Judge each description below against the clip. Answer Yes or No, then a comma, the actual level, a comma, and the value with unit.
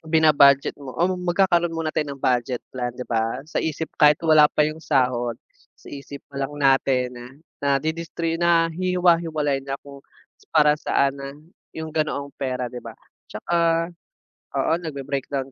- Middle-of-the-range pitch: Yes, medium, 145 Hz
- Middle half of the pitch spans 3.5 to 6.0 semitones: No, average, 3.0 semitones